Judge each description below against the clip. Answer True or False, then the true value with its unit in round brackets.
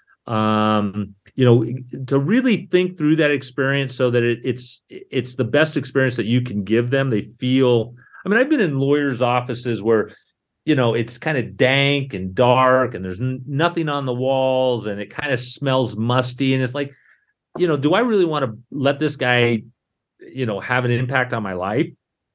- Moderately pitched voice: False (130 Hz)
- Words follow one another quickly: False (195 wpm)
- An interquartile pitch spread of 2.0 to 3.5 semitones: True (2.8 semitones)